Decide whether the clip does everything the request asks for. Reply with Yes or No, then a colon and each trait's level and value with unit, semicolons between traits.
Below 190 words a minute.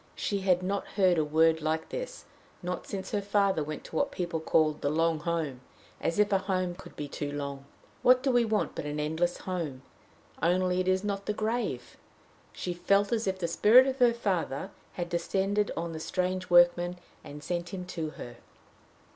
No: average, 195 wpm